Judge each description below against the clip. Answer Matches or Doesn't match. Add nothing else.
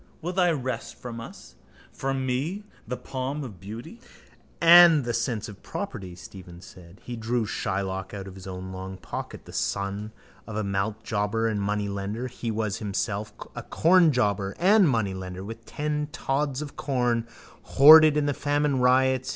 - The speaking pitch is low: Matches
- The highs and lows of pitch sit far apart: Matches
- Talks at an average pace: Matches